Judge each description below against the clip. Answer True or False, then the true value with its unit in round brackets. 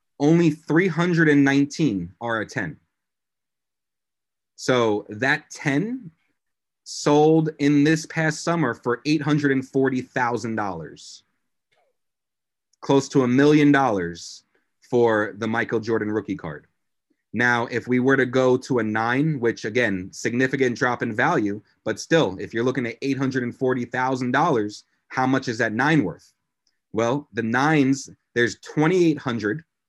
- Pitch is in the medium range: False (130 Hz)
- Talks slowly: True (120 wpm)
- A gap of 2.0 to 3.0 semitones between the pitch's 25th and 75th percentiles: False (3.9 semitones)